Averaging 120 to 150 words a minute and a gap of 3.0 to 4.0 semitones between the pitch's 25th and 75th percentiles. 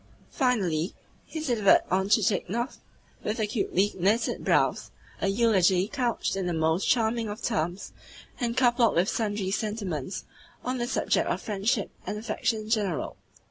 Yes: average, 140 wpm; average, 3.6 semitones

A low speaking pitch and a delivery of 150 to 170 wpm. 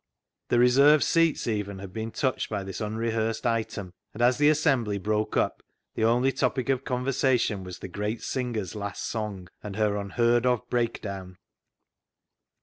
Yes: low, 110 Hz; average, 155 wpm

